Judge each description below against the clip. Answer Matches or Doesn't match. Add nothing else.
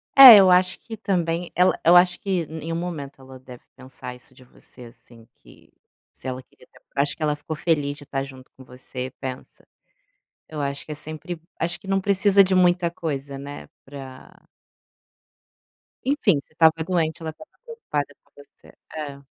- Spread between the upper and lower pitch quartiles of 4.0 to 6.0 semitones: Matches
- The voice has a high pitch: Doesn't match